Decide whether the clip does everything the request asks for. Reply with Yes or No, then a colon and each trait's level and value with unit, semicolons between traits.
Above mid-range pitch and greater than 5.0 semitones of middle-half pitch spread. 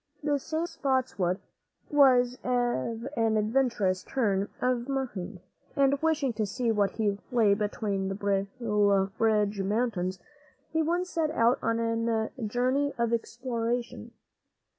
No: high, 230 Hz; average, 4.0 semitones